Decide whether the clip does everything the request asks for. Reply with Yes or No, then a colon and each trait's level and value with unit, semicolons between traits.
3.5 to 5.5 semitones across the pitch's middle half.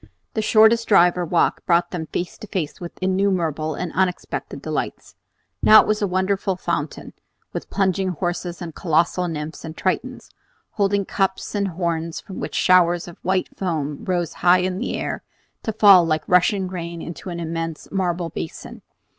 No: narrow, 2.4 semitones